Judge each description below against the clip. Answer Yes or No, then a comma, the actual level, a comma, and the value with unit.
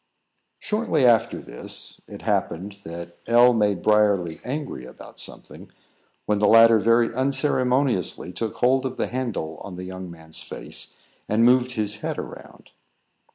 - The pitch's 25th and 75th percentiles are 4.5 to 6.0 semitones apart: Yes, average, 5.2 semitones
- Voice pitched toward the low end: Yes, low, 110 Hz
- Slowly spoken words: No, average, 145 wpm